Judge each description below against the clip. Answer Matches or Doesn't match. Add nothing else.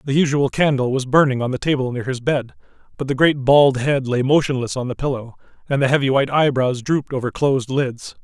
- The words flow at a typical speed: Doesn't match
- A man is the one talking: Matches